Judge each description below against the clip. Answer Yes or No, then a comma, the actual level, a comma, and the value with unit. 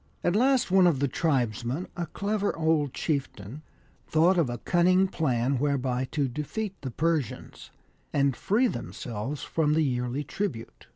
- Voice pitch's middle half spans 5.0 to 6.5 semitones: Yes, wide, 5.4 semitones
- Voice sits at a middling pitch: Yes, medium, 150 Hz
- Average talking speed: Yes, average, 150 wpm